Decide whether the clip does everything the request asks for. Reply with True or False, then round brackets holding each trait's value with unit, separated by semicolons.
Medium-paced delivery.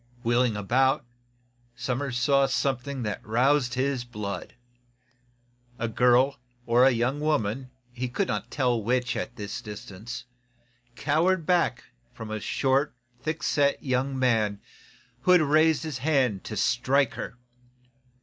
False (130 wpm)